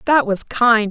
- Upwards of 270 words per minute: No, average, 200 wpm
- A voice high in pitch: Yes, high, 235 Hz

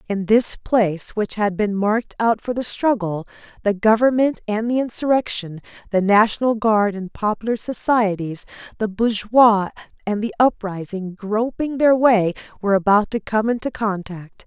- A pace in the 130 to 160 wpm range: Yes, average, 150 wpm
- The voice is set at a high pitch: Yes, high, 215 Hz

